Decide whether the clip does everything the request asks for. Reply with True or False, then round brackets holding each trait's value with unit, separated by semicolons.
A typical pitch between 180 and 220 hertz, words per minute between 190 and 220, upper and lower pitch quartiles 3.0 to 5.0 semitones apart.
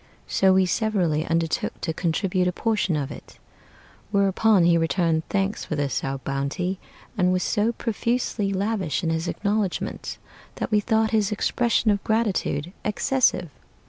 False (190 Hz; 145 wpm; 4.4 semitones)